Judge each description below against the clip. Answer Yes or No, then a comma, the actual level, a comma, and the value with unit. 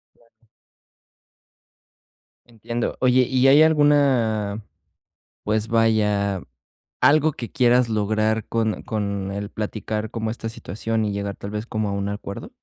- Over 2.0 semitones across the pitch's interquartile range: Yes, narrow, 2.4 semitones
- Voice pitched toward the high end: No, low, 110 Hz